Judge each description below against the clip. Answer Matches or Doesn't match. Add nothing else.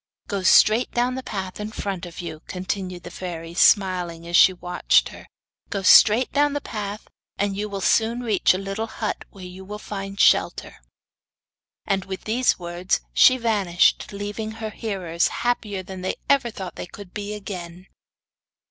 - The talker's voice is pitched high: Matches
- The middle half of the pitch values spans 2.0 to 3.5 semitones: Matches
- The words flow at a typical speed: Matches